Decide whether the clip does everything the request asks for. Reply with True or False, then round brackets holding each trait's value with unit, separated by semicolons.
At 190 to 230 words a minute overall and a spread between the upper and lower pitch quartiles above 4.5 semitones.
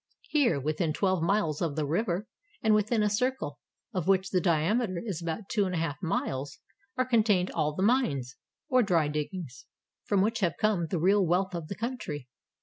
True (200 wpm; 5.1 semitones)